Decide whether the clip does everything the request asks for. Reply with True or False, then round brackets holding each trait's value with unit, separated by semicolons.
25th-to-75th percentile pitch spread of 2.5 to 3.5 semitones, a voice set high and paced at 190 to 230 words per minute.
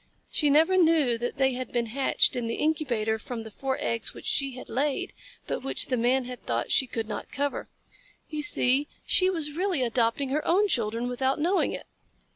False (3.9 semitones; 265 Hz; 200 wpm)